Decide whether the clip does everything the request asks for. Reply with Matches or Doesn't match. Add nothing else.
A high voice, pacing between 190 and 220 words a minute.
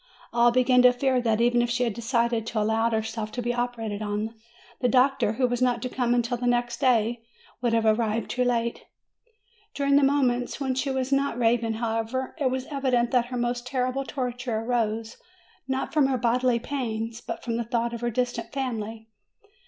Matches